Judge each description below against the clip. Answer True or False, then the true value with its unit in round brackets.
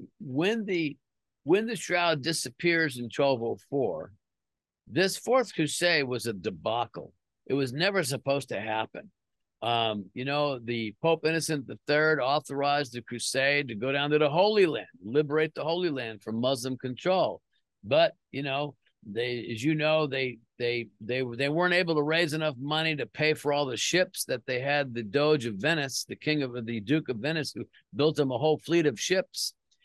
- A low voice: False (145 Hz)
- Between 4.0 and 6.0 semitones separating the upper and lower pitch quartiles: True (4.8 semitones)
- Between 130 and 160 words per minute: False (180 wpm)